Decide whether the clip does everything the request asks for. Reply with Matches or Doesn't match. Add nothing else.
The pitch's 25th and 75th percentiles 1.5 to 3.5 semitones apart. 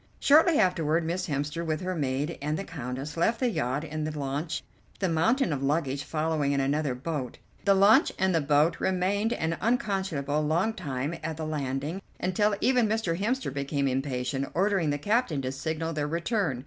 Doesn't match